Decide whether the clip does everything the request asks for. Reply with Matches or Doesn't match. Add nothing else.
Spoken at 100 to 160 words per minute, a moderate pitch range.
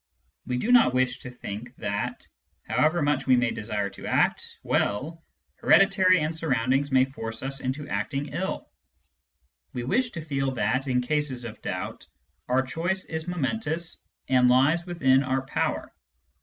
Matches